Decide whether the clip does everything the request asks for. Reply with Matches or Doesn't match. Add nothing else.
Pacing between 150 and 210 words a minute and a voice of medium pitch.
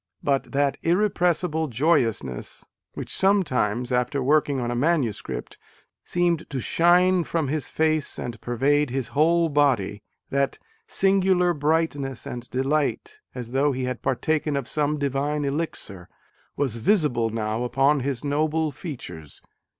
Doesn't match